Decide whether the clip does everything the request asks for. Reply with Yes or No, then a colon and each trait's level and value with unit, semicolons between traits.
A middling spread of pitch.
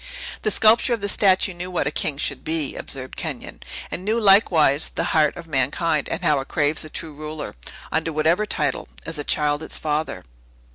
Yes: average, 3.6 semitones